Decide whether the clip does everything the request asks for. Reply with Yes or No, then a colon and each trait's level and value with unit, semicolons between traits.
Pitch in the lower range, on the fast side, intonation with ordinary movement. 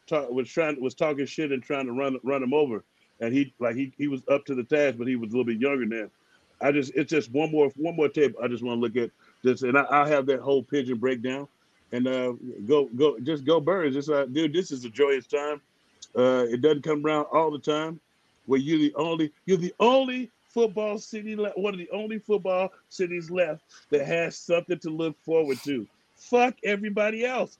No: medium, 145 Hz; fast, 230 wpm; average, 4.3 semitones